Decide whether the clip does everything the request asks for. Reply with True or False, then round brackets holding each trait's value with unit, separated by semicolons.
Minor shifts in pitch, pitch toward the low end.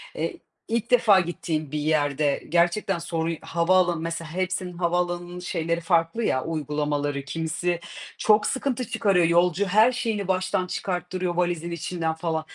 False (2.3 semitones; 175 Hz)